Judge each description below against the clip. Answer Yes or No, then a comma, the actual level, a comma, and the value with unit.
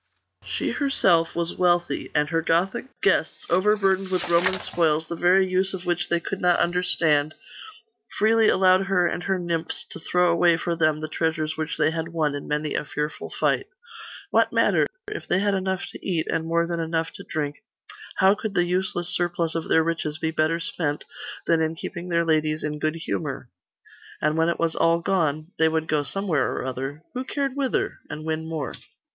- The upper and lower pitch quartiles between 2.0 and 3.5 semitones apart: Yes, narrow, 2.6 semitones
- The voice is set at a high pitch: No, medium, 170 Hz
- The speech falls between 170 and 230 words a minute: Yes, average, 190 wpm